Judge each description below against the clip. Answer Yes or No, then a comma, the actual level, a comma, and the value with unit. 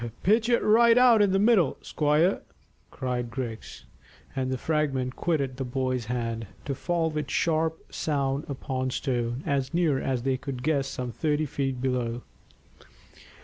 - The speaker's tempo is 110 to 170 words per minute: Yes, average, 155 wpm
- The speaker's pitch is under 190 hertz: Yes, low, 135 Hz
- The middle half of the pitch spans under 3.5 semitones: No, average, 4.1 semitones